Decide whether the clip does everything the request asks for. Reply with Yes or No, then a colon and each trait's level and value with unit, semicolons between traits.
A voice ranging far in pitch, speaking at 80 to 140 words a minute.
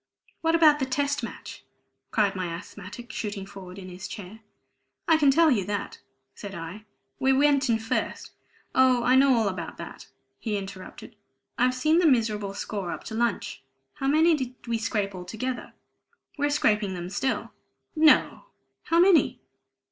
No: wide, 5.7 semitones; average, 165 wpm